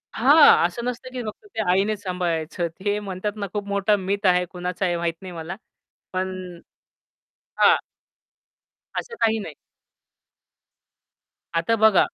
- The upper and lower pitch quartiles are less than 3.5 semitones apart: Yes, average, 3.1 semitones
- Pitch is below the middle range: No, high, 195 Hz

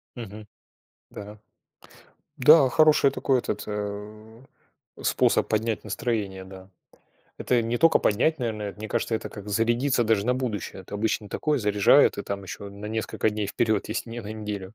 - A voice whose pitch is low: Yes, low, 110 Hz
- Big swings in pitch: No, narrow, 2.6 semitones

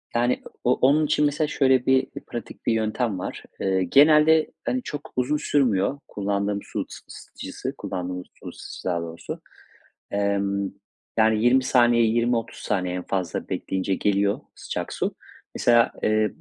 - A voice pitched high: No, low, 115 Hz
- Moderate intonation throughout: Yes, average, 5.0 semitones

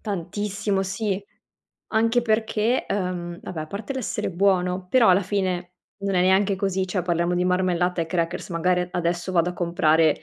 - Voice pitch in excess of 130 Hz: Yes, medium, 185 Hz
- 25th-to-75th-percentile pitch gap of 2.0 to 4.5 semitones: Yes, narrow, 2.3 semitones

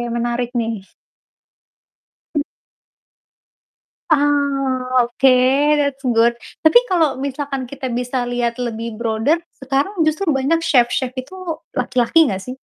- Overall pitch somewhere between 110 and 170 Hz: No, very high, 255 Hz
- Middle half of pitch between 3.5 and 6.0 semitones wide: No, average, 3.0 semitones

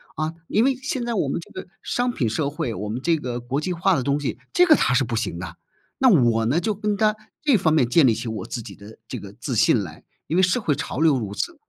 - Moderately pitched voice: Yes, medium, 145 Hz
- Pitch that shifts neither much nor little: No, wide, 9.0 semitones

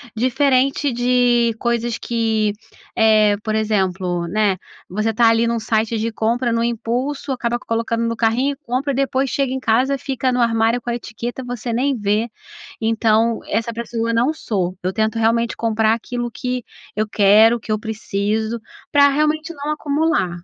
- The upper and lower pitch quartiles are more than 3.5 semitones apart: No, narrow, 2.4 semitones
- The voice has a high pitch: Yes, high, 230 Hz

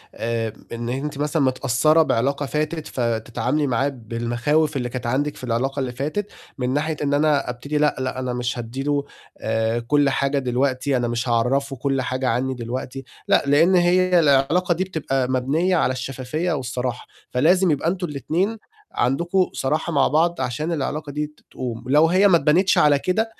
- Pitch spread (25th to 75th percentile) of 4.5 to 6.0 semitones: No, average, 3.5 semitones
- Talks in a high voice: No, medium, 140 Hz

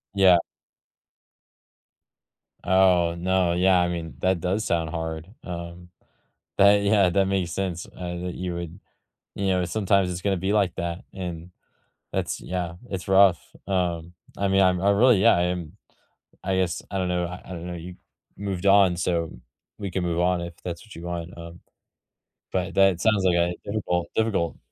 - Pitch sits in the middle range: No, very low, 90 Hz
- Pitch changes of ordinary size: No, narrow, 2.1 semitones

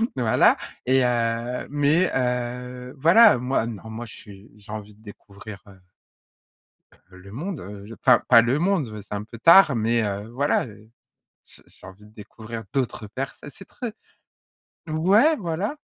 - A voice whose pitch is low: Yes, low, 120 Hz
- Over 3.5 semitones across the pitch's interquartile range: Yes, average, 5.1 semitones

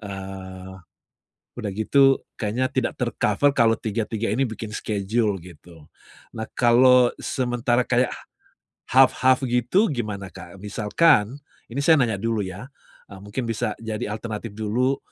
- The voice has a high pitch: No, low, 115 Hz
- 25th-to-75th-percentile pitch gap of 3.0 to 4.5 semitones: Yes, average, 3.5 semitones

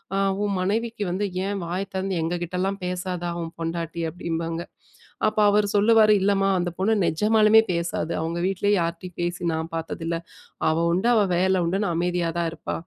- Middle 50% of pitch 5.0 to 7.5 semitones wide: No, average, 3.2 semitones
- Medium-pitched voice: Yes, medium, 180 Hz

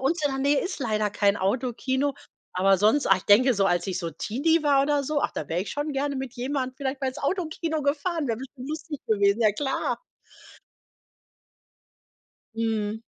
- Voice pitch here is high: Yes, very high, 265 Hz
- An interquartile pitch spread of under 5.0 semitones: No, wide, 5.4 semitones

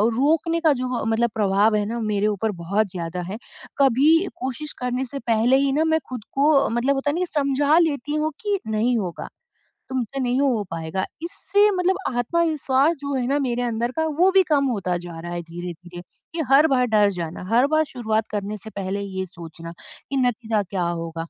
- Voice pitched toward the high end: Yes, high, 245 Hz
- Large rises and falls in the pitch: Yes, wide, 6.0 semitones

